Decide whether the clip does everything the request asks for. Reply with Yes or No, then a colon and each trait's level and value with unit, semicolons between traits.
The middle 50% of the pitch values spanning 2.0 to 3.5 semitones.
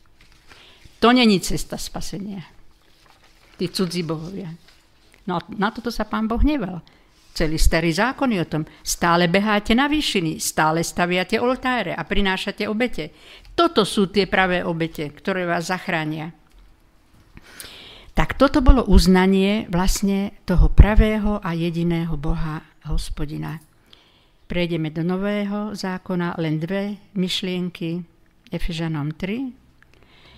No: average, 4.1 semitones